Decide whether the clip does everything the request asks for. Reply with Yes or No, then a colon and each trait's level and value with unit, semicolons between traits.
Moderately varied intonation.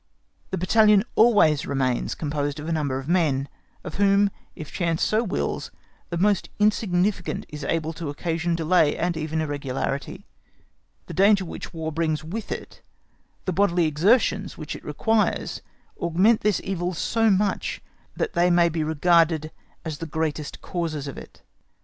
Yes: average, 4.1 semitones